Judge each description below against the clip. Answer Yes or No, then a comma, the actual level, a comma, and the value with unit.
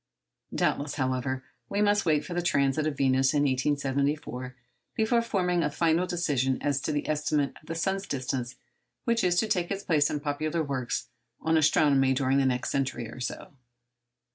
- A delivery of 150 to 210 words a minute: Yes, average, 175 wpm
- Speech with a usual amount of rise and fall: Yes, average, 4.3 semitones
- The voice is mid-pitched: Yes, medium, 145 Hz